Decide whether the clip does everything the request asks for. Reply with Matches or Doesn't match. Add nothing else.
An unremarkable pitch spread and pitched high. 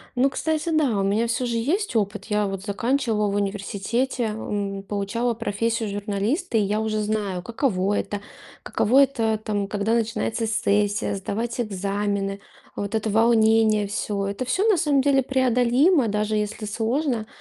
Matches